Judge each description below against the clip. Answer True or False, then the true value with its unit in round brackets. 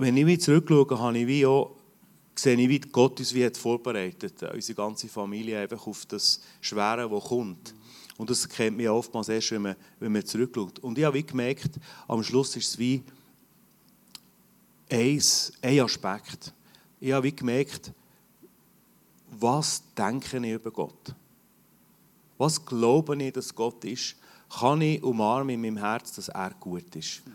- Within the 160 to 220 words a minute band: False (150 wpm)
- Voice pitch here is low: True (125 Hz)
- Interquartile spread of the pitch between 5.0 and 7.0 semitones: False (3.6 semitones)